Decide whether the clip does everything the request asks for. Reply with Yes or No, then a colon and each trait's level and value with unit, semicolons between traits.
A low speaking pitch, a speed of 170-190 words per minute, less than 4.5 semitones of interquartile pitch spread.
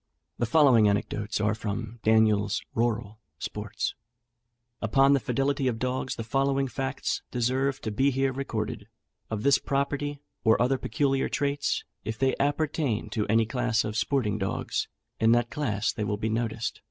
No: low, 120 Hz; average, 155 wpm; average, 3.9 semitones